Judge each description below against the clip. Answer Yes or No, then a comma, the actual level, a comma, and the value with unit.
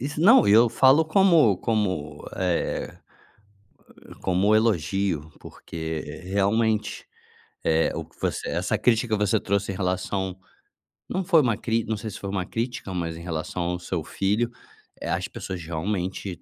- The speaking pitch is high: No, low, 100 Hz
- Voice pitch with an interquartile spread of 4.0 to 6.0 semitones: Yes, average, 4.3 semitones